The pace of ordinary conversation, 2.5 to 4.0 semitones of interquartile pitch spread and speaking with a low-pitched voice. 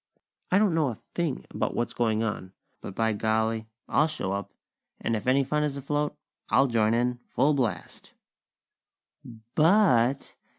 No: average, 155 wpm; average, 5.0 semitones; low, 125 Hz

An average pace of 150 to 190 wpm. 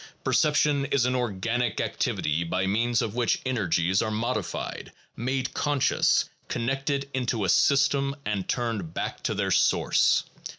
No: slow, 135 wpm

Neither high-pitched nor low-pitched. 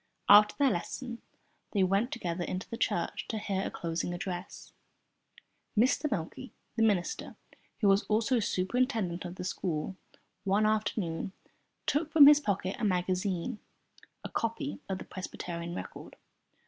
No: high, 200 Hz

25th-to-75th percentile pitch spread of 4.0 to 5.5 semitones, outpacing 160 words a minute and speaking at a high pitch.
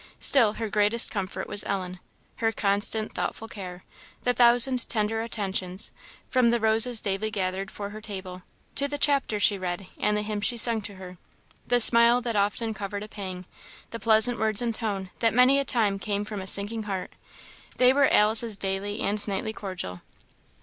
No: average, 2.7 semitones; average, 180 wpm; high, 210 Hz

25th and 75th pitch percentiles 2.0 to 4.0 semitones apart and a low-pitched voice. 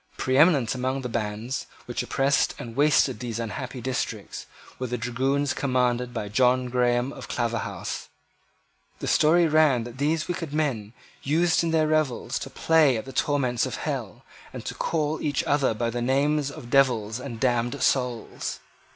Yes: average, 3.2 semitones; low, 130 Hz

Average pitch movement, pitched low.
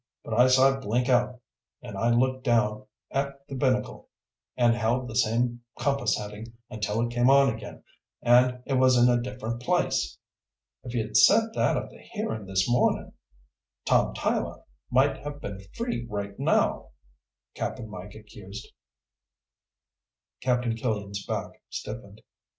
Yes: average, 3.0 semitones; low, 120 Hz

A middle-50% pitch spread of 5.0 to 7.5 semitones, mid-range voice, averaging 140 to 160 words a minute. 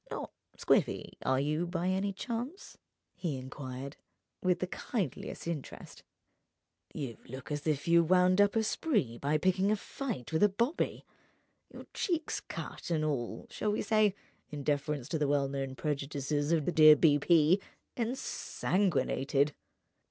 Yes: wide, 5.5 semitones; medium, 160 Hz; average, 145 wpm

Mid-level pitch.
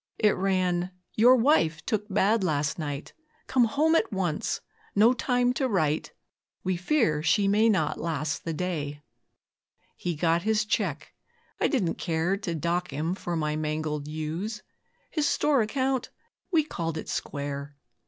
Yes: medium, 180 Hz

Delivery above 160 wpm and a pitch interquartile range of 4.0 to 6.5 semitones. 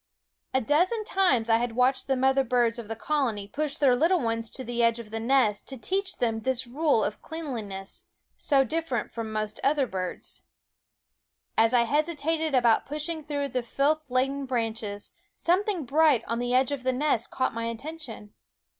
Yes: average, 180 wpm; average, 4.7 semitones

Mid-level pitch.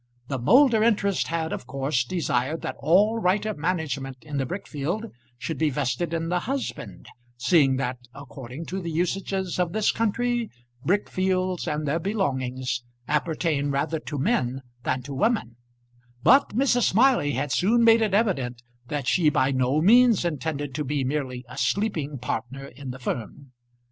Yes: medium, 155 Hz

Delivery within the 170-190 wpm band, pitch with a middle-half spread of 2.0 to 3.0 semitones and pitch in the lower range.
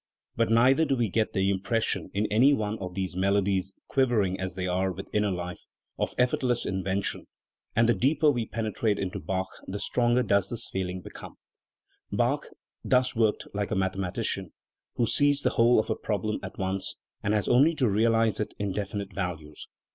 No: average, 180 wpm; average, 3.7 semitones; low, 105 Hz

